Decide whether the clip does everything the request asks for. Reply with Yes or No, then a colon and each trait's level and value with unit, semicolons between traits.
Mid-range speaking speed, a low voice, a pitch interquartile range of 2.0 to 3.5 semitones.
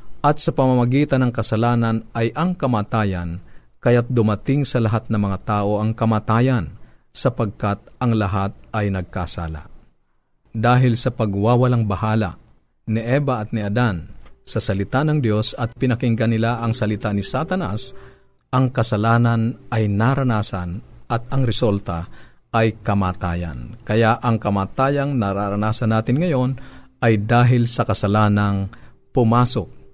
Yes: average, 125 wpm; low, 115 Hz; average, 3.2 semitones